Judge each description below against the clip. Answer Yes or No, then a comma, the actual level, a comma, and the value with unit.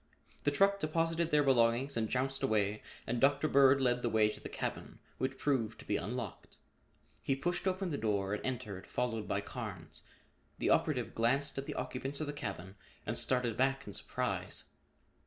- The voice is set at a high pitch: No, low, 125 Hz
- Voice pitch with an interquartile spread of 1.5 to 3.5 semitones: No, average, 4.3 semitones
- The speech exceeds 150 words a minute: Yes, average, 180 wpm